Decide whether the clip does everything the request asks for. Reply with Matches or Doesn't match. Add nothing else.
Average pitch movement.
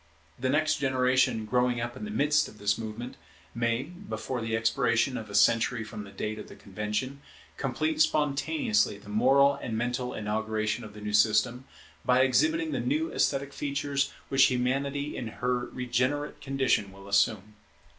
Matches